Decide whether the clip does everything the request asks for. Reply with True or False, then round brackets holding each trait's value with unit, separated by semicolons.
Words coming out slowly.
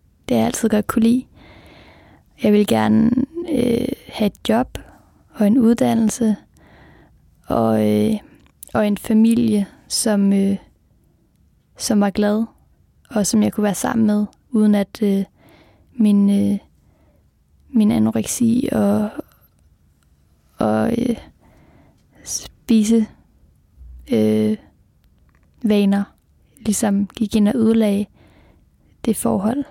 True (105 wpm)